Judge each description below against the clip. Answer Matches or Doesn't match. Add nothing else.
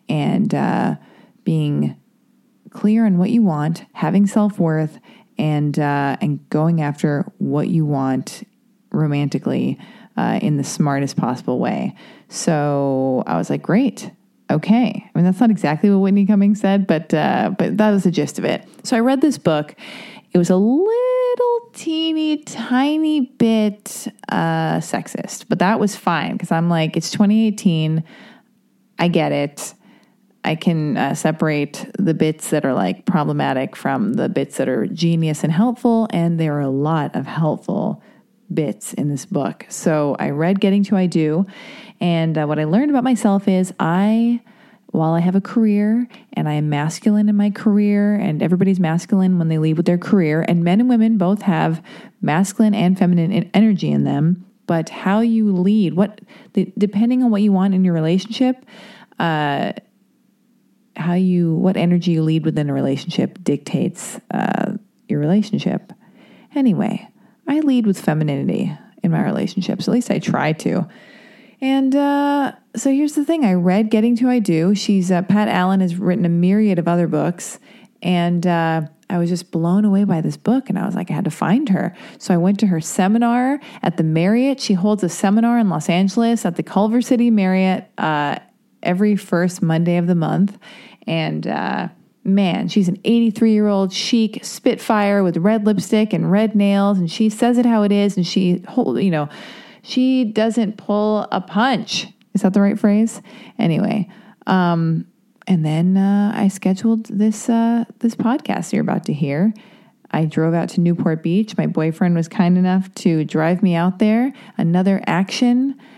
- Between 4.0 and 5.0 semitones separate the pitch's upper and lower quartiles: Matches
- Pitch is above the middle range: Matches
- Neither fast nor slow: Matches